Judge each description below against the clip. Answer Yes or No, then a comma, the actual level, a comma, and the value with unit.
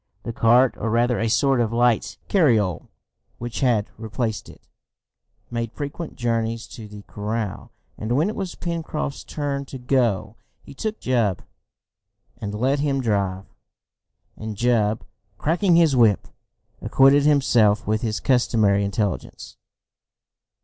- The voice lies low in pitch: Yes, low, 115 Hz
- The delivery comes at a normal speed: No, slow, 130 wpm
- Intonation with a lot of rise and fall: No, average, 4.3 semitones